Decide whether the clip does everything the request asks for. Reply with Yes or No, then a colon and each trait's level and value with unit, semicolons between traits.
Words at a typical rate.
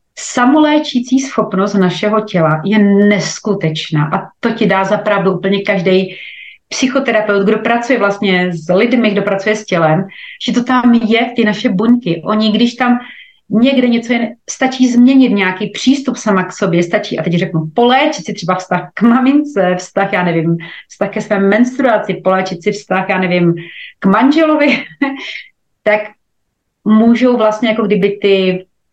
Yes: average, 150 wpm